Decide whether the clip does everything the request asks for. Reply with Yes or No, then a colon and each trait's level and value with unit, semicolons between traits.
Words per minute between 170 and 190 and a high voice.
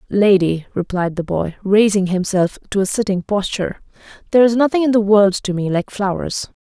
Yes: average, 180 wpm; high, 200 Hz